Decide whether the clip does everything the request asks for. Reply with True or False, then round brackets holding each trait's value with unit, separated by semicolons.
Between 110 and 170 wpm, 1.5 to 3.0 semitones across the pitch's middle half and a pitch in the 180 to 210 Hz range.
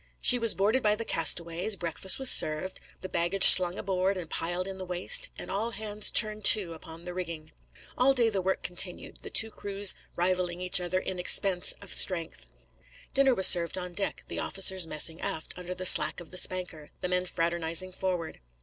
False (195 wpm; 2.4 semitones; 185 Hz)